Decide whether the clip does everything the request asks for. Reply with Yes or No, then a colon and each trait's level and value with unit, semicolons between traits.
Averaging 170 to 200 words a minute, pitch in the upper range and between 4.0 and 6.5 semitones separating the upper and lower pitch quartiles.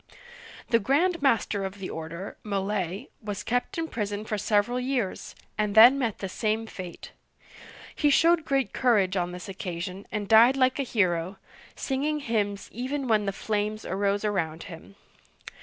No: average, 155 wpm; high, 210 Hz; average, 4.5 semitones